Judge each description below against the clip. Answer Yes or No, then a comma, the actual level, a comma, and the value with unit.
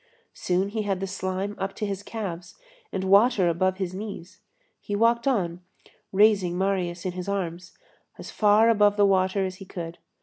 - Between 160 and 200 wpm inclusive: Yes, average, 175 wpm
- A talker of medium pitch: No, high, 195 Hz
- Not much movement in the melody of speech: Yes, narrow, 2.0 semitones